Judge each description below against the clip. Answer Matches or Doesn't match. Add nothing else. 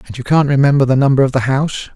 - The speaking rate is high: Matches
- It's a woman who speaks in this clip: Doesn't match